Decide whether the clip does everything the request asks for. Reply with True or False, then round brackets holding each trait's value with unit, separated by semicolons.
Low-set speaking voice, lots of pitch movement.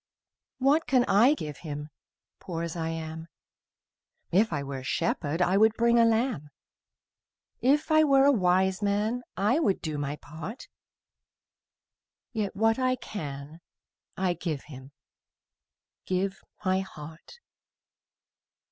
False (190 Hz; 6.8 semitones)